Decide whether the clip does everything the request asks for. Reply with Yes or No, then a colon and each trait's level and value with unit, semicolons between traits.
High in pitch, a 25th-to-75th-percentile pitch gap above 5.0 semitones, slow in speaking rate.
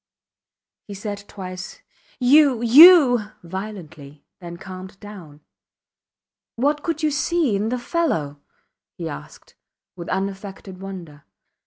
Yes: high, 200 Hz; wide, 5.6 semitones; slow, 110 wpm